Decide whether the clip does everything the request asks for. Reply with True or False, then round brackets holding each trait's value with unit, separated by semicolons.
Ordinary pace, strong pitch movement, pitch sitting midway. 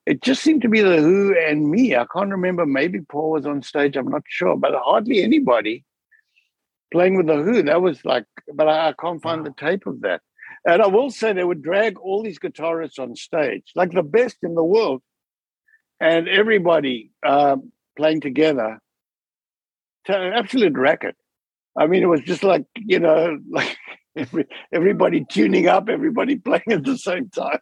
True (180 wpm; 6.1 semitones; 175 Hz)